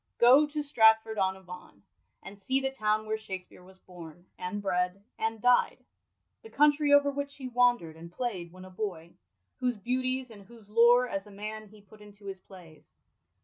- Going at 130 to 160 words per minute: No, average, 190 wpm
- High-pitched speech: Yes, high, 215 Hz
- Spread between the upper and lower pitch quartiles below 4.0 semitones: No, average, 4.8 semitones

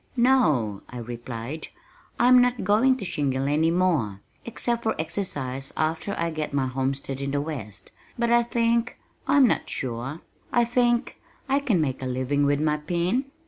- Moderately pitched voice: Yes, medium, 155 Hz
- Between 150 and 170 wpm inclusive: Yes, average, 165 wpm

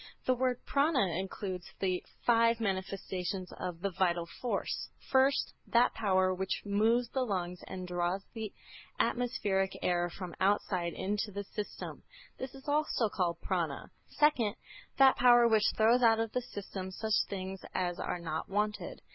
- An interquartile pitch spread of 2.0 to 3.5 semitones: No, average, 4.2 semitones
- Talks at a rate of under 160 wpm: Yes, average, 150 wpm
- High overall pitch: Yes, high, 200 Hz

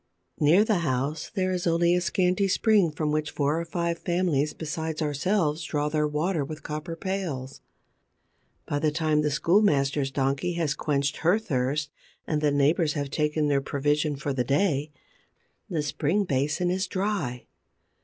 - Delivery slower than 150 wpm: No, average, 165 wpm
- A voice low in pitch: No, medium, 155 Hz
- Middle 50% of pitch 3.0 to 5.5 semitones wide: Yes, average, 3.3 semitones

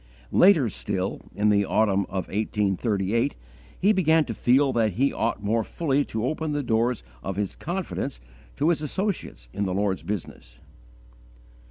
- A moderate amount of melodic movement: No, wide, 6.4 semitones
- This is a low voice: Yes, low, 110 Hz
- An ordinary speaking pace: Yes, average, 155 wpm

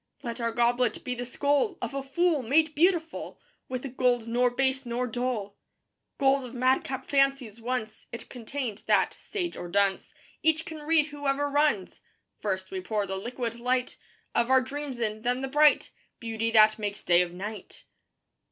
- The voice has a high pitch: Yes, very high, 250 Hz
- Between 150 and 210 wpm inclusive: Yes, average, 170 wpm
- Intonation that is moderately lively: Yes, average, 3.8 semitones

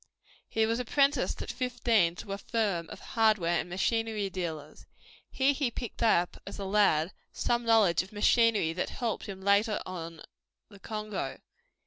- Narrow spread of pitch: No, average, 4.2 semitones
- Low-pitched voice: No, high, 210 Hz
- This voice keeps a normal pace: Yes, average, 155 wpm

